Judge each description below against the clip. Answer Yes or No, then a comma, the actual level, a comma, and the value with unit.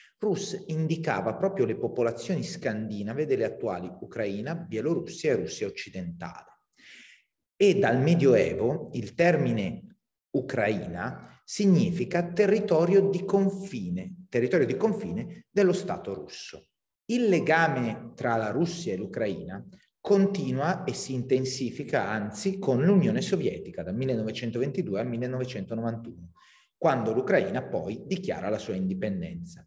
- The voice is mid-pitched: Yes, medium, 170 Hz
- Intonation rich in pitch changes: Yes, wide, 7.6 semitones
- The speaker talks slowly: Yes, slow, 110 wpm